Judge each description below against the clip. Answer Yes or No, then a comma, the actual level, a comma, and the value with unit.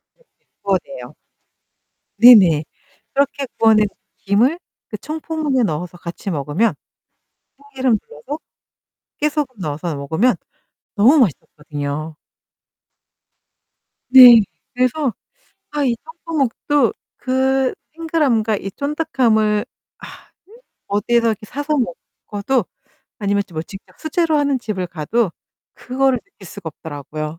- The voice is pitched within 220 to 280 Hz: Yes, high, 235 Hz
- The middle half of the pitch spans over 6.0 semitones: Yes, wide, 7.1 semitones